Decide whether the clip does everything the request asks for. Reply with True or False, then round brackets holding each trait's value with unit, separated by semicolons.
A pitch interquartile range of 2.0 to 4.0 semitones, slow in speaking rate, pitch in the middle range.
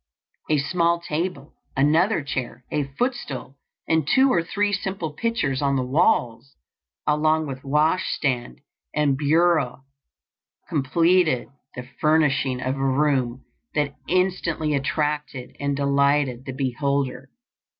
True (3.4 semitones; 120 wpm; 145 Hz)